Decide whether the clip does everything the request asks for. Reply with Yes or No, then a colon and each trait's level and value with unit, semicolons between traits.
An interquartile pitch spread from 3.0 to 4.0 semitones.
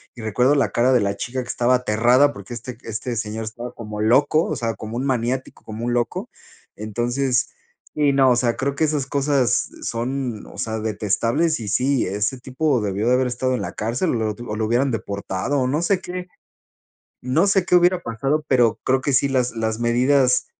Yes: average, 3.5 semitones